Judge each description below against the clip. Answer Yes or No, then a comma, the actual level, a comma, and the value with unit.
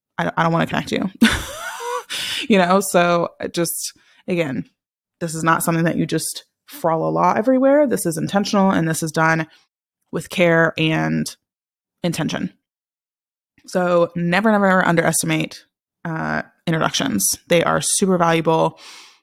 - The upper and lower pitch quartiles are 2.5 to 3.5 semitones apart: No, average, 4.0 semitones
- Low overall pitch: No, medium, 170 Hz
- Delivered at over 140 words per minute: No, slow, 135 wpm